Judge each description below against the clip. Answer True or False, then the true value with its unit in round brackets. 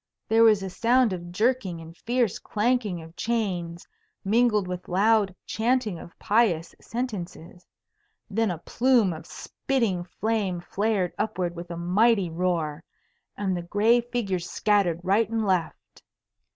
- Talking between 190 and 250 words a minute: False (140 wpm)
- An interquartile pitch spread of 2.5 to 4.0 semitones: False (4.4 semitones)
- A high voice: True (200 Hz)